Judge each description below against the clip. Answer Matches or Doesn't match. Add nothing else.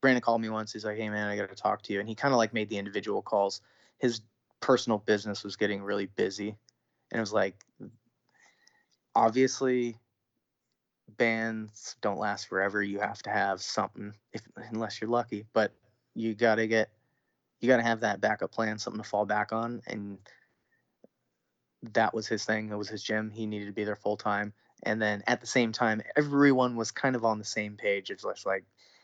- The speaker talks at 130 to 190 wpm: Doesn't match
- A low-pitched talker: Matches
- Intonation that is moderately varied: Doesn't match